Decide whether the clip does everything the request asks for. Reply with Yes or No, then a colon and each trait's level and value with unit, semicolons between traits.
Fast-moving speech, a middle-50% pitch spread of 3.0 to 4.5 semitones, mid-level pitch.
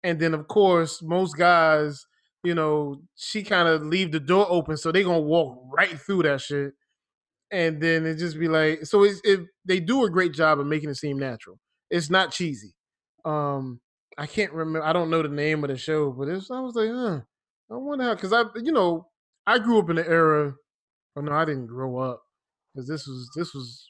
Yes: fast, 220 wpm; average, 4.1 semitones; medium, 165 Hz